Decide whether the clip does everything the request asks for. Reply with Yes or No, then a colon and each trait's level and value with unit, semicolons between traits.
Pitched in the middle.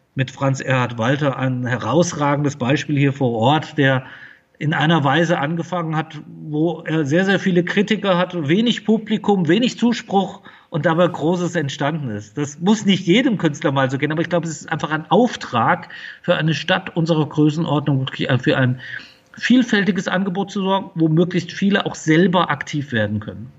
Yes: medium, 165 Hz